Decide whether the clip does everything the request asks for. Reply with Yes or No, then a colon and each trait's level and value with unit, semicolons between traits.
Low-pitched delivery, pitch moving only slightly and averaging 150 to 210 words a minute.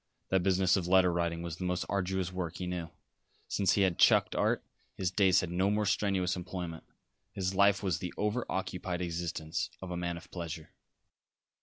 Yes: very low, 90 Hz; narrow, 1.6 semitones; average, 185 wpm